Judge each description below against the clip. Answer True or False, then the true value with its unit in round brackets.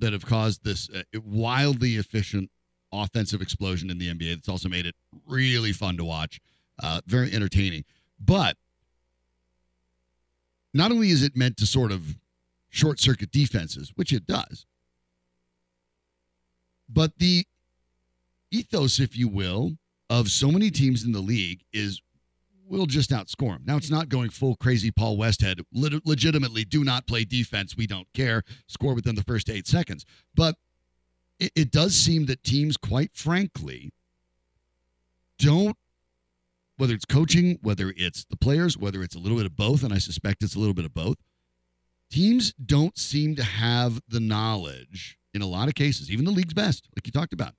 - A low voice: True (105 Hz)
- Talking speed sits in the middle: True (165 wpm)